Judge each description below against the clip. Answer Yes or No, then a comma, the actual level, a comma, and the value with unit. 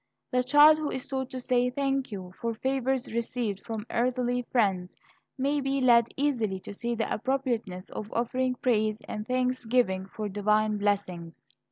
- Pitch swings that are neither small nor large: Yes, average, 3.5 semitones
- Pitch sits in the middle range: No, high, 240 Hz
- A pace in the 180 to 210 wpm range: No, average, 160 wpm